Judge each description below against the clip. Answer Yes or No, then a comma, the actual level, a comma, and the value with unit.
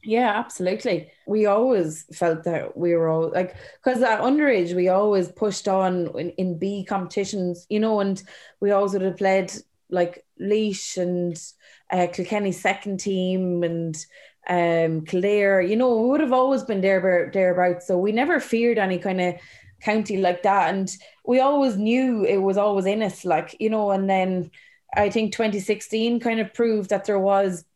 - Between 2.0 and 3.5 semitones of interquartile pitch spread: Yes, average, 2.9 semitones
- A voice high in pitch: Yes, high, 195 Hz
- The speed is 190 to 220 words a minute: No, average, 175 wpm